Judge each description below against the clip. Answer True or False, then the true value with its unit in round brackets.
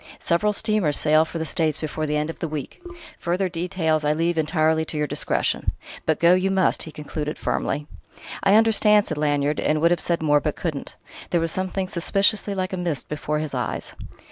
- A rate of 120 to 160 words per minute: False (200 wpm)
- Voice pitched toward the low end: False (160 Hz)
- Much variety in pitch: False (3.3 semitones)